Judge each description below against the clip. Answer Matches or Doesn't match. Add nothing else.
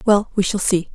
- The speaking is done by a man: Doesn't match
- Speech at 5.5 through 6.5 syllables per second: Doesn't match